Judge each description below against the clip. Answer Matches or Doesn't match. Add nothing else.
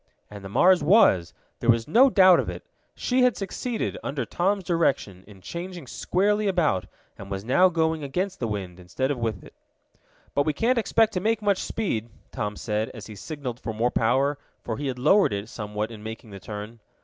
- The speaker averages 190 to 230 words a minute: Matches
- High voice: Doesn't match